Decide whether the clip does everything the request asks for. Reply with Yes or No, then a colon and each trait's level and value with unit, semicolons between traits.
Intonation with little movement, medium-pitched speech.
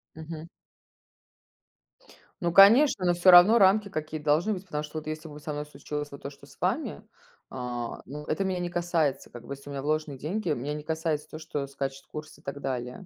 No: average, 3.6 semitones; medium, 155 Hz